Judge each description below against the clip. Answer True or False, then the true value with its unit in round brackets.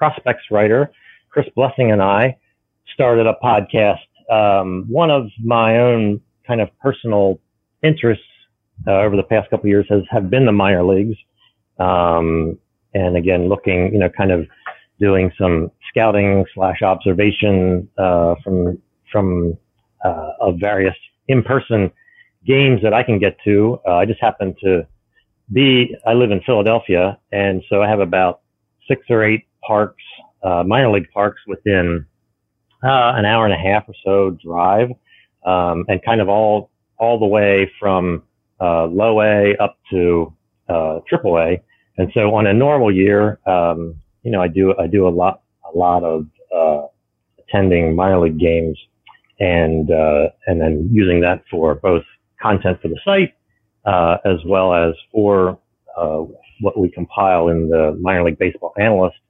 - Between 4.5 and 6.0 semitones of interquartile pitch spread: False (3.5 semitones)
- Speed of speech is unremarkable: True (160 wpm)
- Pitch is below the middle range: True (100 Hz)